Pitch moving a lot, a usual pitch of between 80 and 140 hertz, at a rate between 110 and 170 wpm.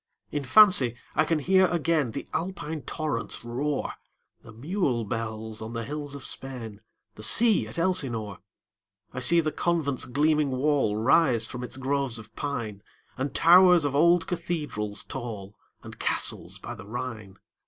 Yes: wide, 5.8 semitones; low, 135 Hz; average, 155 wpm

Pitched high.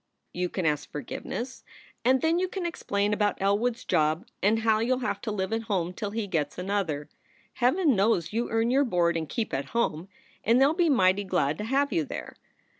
Yes: high, 210 Hz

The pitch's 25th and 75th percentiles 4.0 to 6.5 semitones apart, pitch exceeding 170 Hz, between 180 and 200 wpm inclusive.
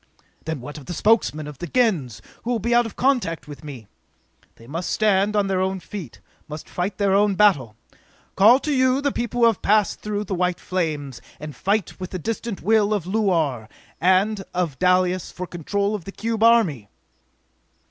Yes: average, 5.1 semitones; high, 190 Hz; average, 190 wpm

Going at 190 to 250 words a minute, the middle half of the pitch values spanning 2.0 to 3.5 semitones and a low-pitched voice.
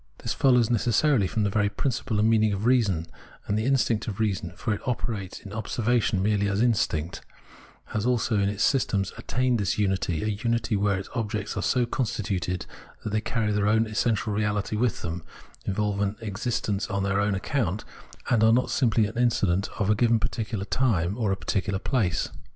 Yes: average, 195 wpm; average, 2.7 semitones; low, 105 Hz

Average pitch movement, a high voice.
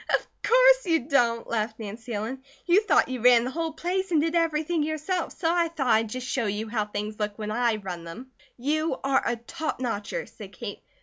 No: wide, 6.8 semitones; very high, 255 Hz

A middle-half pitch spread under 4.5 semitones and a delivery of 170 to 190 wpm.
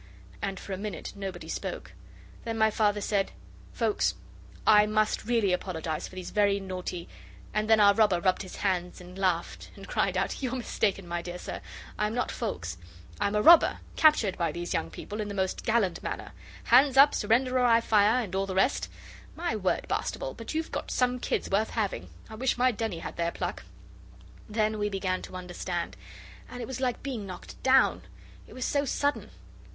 No: average, 4.1 semitones; average, 200 wpm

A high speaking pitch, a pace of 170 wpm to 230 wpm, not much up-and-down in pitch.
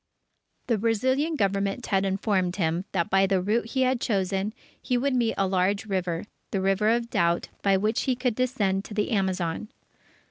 No: high, 200 Hz; average, 180 wpm; average, 3.5 semitones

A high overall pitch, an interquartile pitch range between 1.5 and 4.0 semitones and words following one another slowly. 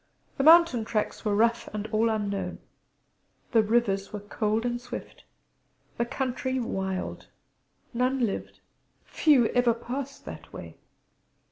Yes: high, 235 Hz; average, 3.1 semitones; slow, 125 wpm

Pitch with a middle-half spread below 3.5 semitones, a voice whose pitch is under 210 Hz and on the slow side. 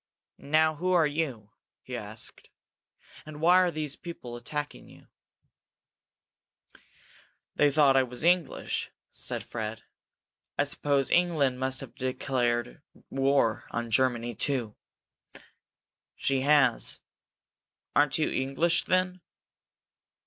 No: average, 4.0 semitones; medium, 140 Hz; slow, 105 wpm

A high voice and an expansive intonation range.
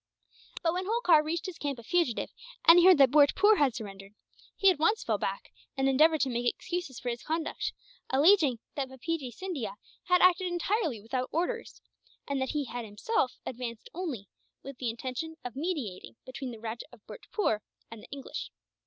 Yes: very high, 280 Hz; wide, 6.3 semitones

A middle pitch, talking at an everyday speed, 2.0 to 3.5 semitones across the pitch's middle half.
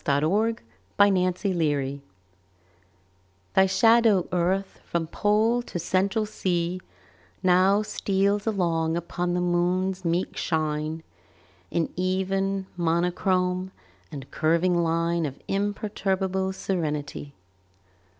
No: medium, 180 Hz; slow, 95 wpm; narrow, 2.5 semitones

